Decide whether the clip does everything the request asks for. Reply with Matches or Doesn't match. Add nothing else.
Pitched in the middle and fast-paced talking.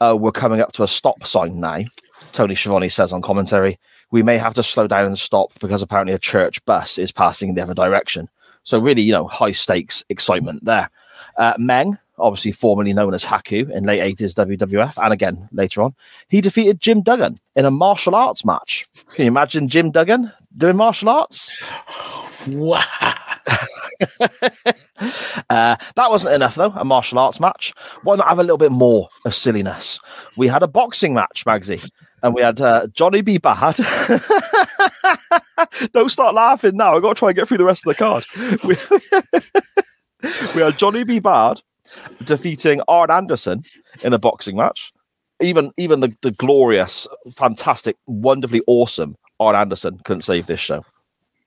Doesn't match